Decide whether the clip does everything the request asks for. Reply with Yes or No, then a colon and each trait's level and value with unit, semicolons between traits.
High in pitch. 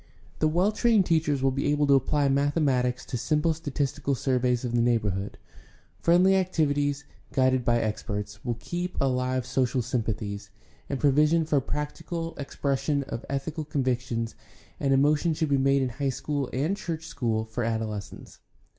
No: low, 135 Hz